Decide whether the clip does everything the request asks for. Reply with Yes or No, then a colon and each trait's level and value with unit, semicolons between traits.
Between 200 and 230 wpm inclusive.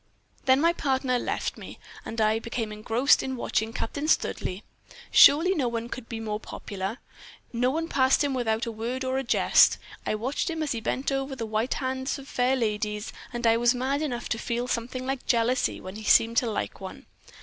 Yes: fast, 205 wpm